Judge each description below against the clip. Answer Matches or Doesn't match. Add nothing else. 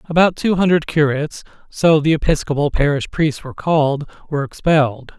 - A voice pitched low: Doesn't match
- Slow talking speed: Matches